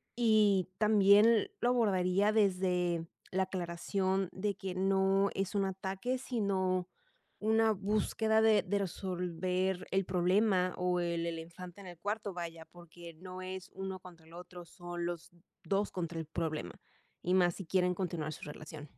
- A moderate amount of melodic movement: No, narrow, 2.3 semitones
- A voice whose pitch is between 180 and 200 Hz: Yes, medium, 185 Hz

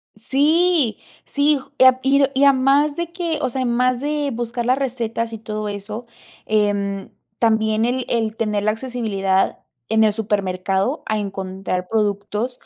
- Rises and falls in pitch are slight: No, average, 4.2 semitones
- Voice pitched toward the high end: Yes, high, 230 Hz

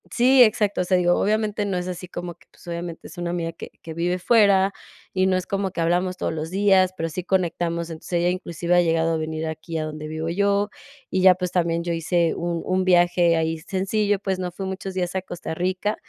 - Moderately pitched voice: Yes, medium, 180 Hz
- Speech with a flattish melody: Yes, narrow, 2.1 semitones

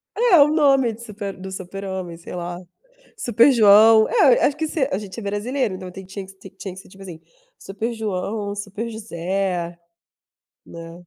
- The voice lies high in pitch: Yes, high, 200 Hz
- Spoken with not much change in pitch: No, average, 3.7 semitones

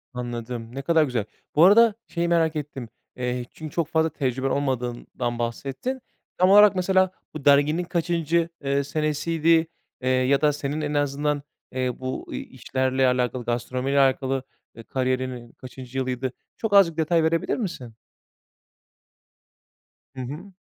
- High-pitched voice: No, medium, 140 Hz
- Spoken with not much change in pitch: No, average, 4.1 semitones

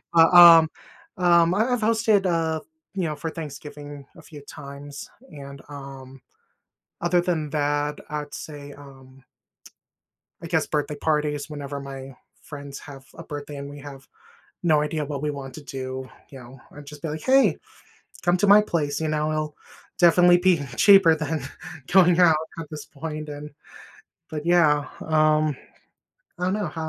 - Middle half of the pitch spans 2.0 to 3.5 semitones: Yes, average, 2.7 semitones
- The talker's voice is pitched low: No, medium, 150 Hz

